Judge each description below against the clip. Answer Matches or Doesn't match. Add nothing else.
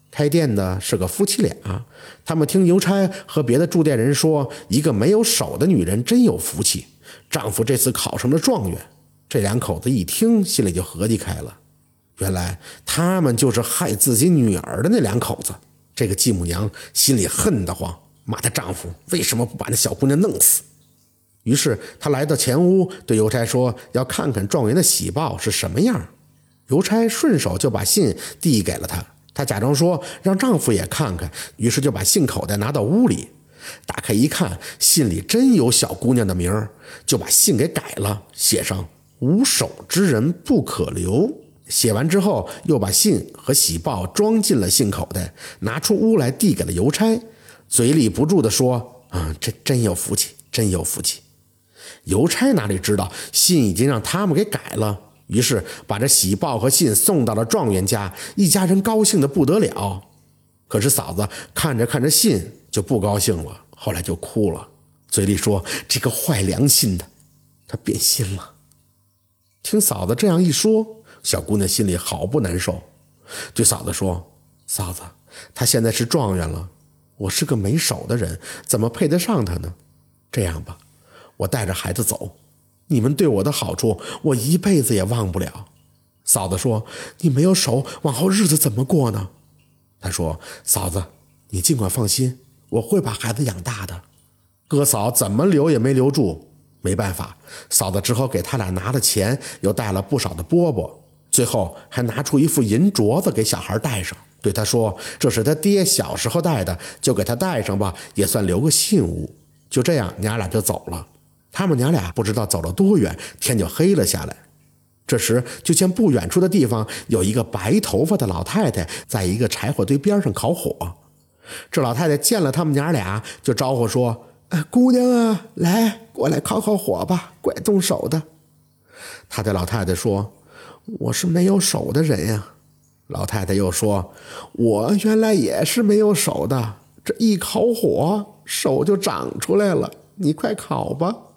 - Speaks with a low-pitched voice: Matches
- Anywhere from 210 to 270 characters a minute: Matches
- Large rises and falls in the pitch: Matches